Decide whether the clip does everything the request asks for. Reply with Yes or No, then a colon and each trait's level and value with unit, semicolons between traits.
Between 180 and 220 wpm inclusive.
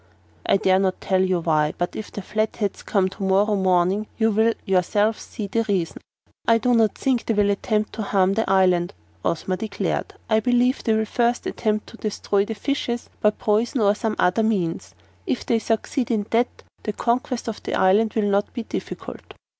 Yes: average, 195 wpm